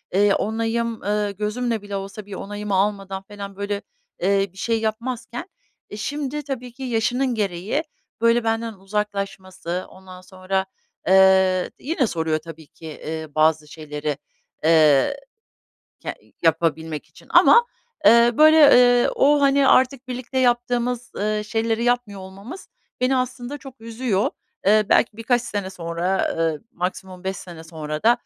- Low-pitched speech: No, high, 210 Hz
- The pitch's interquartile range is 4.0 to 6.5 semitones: Yes, average, 4.6 semitones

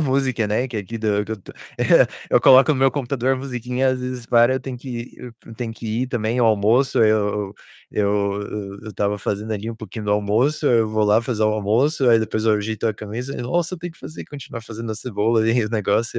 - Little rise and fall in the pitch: No, average, 3.0 semitones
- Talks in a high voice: No, low, 115 Hz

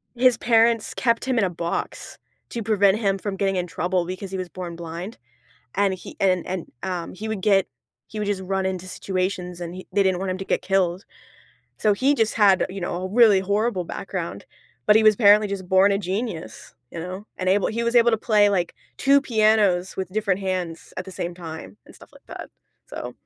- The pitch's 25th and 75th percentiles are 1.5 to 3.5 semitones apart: Yes, average, 2.7 semitones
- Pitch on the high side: Yes, high, 195 Hz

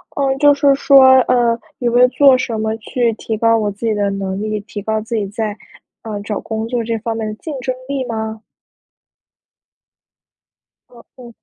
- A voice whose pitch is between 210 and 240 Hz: Yes, high, 225 Hz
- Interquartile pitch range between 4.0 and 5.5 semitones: No, narrow, 2.5 semitones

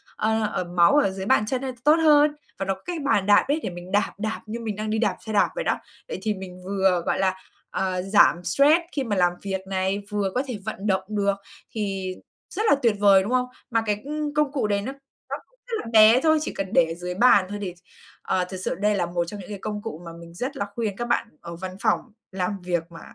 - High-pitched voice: Yes, high, 205 Hz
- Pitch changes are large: No, average, 4.2 semitones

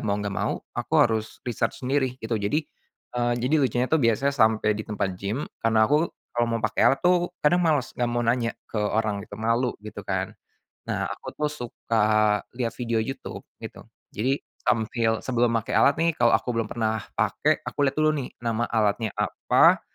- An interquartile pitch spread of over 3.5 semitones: No, average, 2.8 semitones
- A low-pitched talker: Yes, low, 120 Hz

